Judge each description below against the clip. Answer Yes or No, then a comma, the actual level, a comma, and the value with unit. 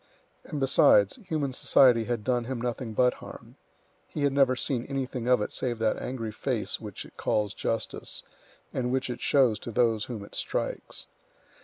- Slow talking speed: No, average, 175 wpm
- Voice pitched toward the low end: Yes, low, 125 Hz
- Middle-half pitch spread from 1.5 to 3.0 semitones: Yes, narrow, 2.6 semitones